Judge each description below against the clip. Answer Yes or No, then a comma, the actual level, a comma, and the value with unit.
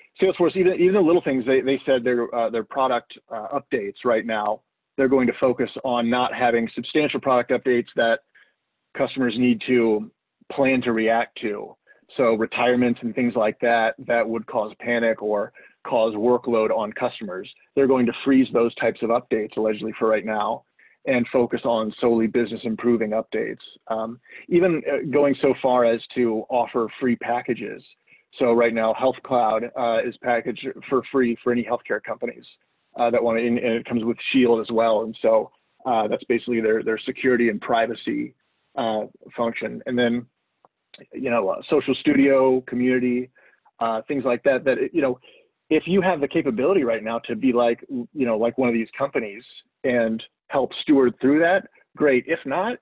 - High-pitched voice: No, low, 120 Hz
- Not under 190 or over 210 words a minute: No, average, 180 wpm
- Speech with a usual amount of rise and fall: No, narrow, 2.3 semitones